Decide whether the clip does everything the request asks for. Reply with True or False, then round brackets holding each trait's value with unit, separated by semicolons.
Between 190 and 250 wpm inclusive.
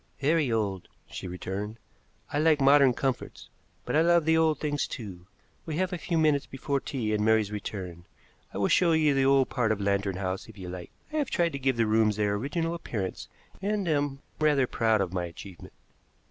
True (200 wpm)